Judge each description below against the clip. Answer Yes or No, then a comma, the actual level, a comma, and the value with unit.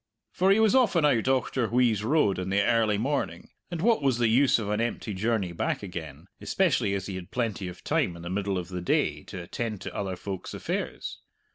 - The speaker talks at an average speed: No, fast, 215 wpm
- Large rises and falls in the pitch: Yes, wide, 5.7 semitones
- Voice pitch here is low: Yes, low, 110 Hz